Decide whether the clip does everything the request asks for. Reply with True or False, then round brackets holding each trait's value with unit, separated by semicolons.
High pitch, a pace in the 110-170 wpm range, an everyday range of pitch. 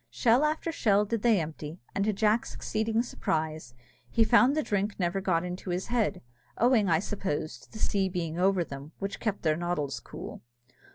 False (195 Hz; 185 wpm; 4.9 semitones)